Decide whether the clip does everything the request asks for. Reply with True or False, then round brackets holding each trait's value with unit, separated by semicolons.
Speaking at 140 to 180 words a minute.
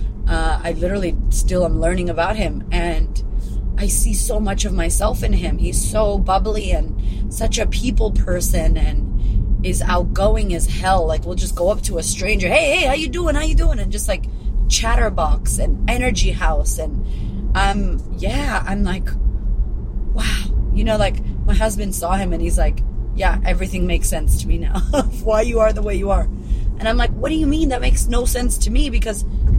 False (195 wpm)